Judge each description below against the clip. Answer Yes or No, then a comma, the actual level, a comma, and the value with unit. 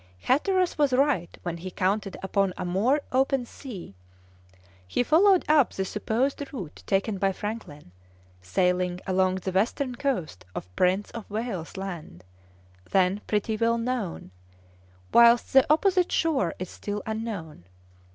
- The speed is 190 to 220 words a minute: No, slow, 135 wpm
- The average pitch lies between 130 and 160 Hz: No, high, 210 Hz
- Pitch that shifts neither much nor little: No, wide, 5.8 semitones